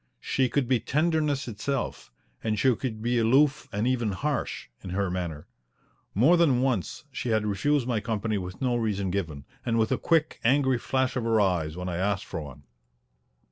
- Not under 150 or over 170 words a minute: No, average, 185 wpm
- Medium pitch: No, low, 115 Hz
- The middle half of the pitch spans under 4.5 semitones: No, average, 5.2 semitones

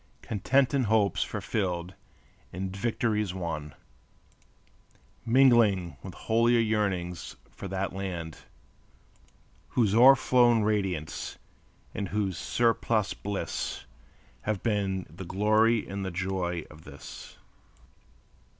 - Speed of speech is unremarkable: No, slow, 100 wpm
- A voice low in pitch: Yes, low, 100 Hz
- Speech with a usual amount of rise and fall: Yes, average, 3.6 semitones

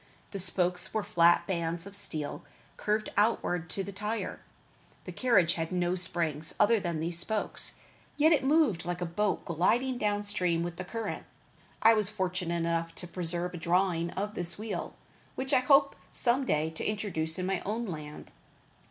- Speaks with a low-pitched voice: No, medium, 185 Hz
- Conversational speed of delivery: Yes, average, 175 wpm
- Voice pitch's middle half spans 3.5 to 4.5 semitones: Yes, average, 3.9 semitones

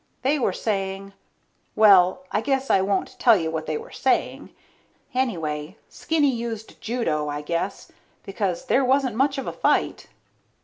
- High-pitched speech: Yes, high, 215 Hz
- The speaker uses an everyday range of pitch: No, wide, 6.3 semitones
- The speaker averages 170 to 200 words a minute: No, average, 150 wpm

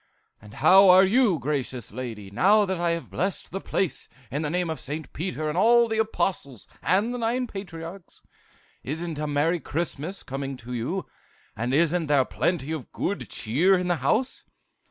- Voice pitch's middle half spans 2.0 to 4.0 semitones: No, wide, 5.4 semitones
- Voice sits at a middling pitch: Yes, medium, 165 Hz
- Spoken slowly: No, average, 175 wpm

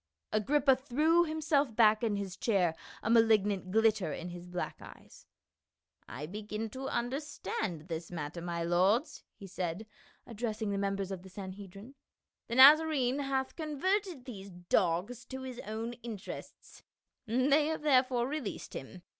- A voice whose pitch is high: Yes, high, 220 Hz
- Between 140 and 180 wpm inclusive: Yes, average, 155 wpm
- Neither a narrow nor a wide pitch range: No, wide, 6.0 semitones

